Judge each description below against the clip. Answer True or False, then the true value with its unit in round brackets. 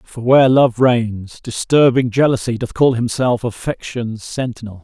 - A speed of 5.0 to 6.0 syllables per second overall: False (4.4 syllables/s)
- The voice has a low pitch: True (120 Hz)